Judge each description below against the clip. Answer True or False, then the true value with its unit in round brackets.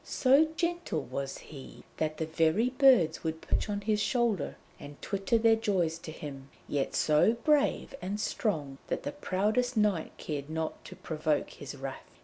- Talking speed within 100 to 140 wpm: False (165 wpm)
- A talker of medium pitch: True (180 Hz)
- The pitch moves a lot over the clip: True (6.8 semitones)